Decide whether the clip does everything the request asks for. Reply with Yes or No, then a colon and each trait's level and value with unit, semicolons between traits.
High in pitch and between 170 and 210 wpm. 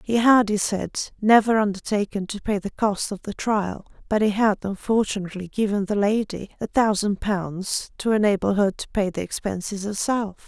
Yes: high, 205 Hz; average, 180 wpm